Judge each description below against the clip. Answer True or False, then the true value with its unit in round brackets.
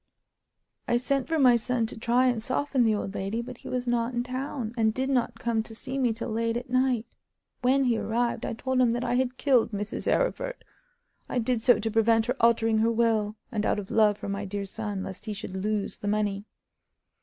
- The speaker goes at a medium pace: False (225 wpm)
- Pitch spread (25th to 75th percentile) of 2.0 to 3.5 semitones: True (2.6 semitones)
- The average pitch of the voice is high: True (230 Hz)